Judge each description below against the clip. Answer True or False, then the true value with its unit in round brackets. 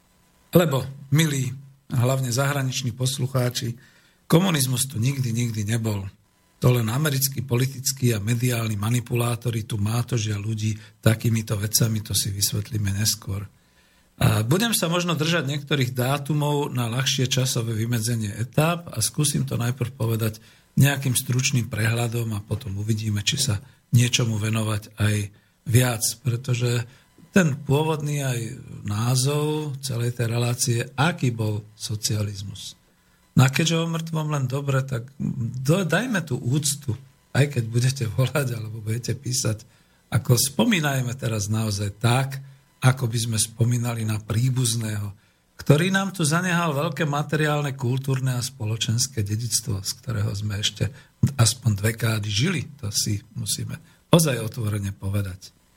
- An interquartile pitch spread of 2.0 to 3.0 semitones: False (3.8 semitones)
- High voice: False (120 Hz)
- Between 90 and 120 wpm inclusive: False (130 wpm)